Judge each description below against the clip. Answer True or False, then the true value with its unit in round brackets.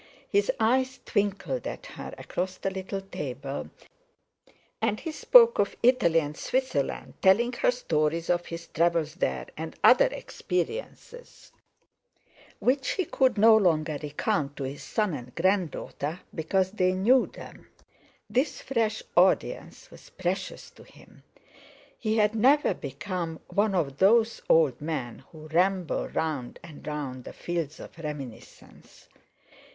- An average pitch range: False (6.4 semitones)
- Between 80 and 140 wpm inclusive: True (135 wpm)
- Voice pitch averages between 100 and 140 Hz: False (185 Hz)